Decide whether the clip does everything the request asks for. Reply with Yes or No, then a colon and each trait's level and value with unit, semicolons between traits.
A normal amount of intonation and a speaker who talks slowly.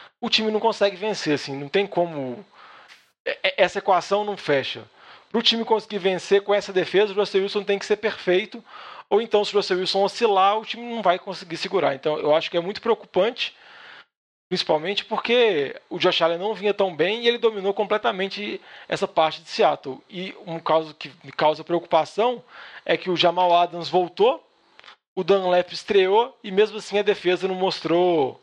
No: average, 3.5 semitones; fast, 185 wpm